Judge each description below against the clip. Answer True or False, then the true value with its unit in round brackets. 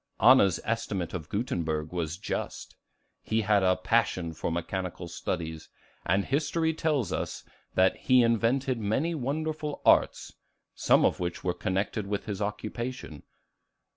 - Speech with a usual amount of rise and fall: False (6.3 semitones)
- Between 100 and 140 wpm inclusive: True (135 wpm)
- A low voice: True (105 Hz)